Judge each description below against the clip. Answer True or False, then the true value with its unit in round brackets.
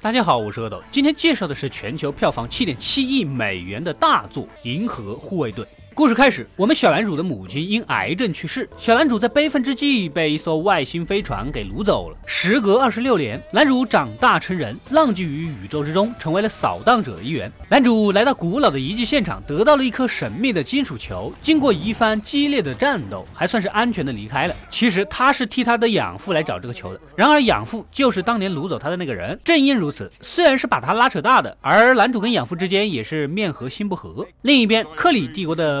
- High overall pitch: True (215 Hz)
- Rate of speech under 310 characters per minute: False (335 characters per minute)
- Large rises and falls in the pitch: True (8.0 semitones)